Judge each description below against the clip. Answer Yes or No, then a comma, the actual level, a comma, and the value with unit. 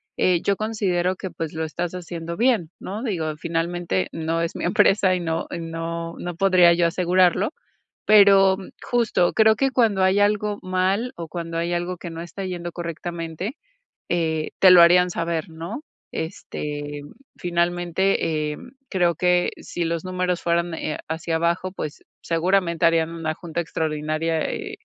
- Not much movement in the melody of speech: Yes, narrow, 2.1 semitones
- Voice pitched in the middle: Yes, medium, 175 Hz